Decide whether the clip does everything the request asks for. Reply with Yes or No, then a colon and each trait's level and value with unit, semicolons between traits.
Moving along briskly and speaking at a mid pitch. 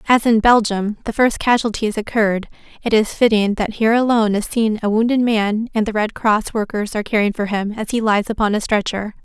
No: fast, 215 wpm; high, 215 Hz